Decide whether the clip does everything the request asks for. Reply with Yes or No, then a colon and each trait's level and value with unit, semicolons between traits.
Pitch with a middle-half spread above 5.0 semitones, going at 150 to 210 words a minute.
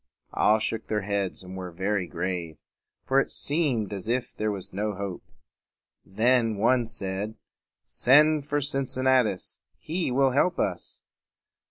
No: wide, 5.5 semitones; average, 140 wpm